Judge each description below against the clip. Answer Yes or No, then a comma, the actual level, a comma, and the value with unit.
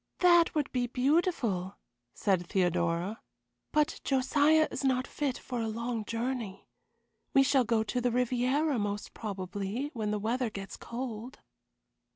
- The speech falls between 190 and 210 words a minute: No, average, 140 wpm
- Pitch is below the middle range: No, high, 240 Hz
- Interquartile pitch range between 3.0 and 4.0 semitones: No, average, 4.4 semitones